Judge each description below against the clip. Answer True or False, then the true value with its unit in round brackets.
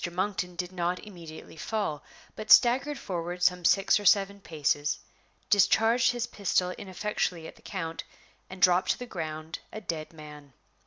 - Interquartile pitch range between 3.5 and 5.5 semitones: True (3.9 semitones)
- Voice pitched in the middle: True (180 Hz)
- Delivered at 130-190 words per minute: True (155 wpm)